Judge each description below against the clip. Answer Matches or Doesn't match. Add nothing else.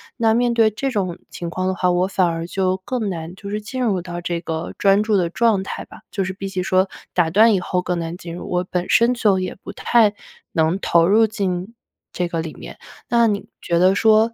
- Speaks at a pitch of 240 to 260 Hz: Doesn't match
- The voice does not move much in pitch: Doesn't match